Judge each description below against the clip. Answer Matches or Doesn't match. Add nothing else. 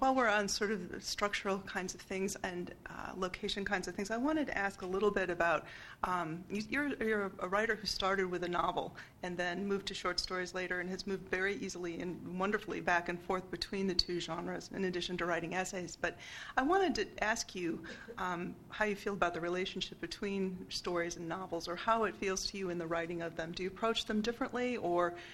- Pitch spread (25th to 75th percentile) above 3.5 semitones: Doesn't match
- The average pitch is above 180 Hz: Matches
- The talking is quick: Matches